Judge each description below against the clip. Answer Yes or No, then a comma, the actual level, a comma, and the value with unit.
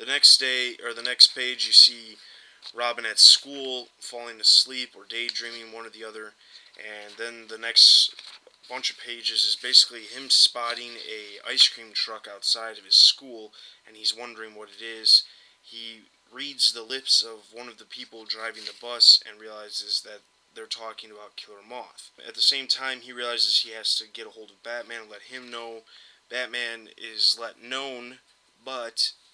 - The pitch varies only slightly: Yes, narrow, 1.8 semitones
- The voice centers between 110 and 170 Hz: Yes, low, 115 Hz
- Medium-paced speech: Yes, average, 180 wpm